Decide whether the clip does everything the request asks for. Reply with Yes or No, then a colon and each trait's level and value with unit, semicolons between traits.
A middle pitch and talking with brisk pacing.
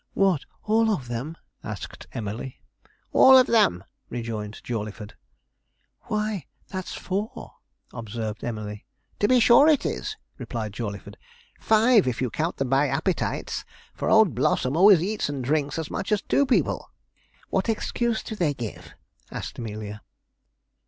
No: medium, 145 Hz; average, 140 wpm